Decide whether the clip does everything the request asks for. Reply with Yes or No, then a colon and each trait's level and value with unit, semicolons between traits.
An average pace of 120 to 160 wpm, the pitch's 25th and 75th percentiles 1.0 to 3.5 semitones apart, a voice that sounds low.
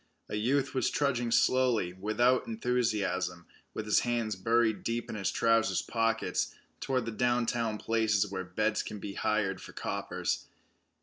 Yes: average, 145 wpm; narrow, 2.5 semitones; low, 115 Hz